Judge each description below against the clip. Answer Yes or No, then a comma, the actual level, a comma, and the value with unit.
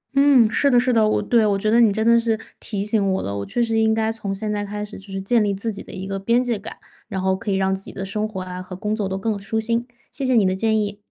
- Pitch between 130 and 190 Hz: No, high, 210 Hz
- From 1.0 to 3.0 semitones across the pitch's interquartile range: Yes, narrow, 2.6 semitones